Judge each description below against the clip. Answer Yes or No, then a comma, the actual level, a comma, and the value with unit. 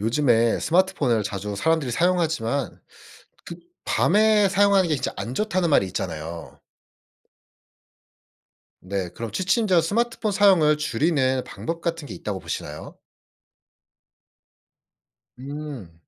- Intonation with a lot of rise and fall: Yes, wide, 8.3 semitones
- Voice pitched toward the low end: No, medium, 150 Hz